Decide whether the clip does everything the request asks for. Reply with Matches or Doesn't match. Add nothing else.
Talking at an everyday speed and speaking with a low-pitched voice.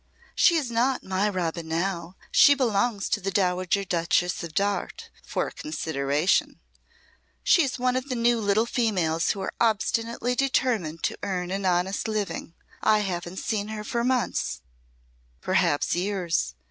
Doesn't match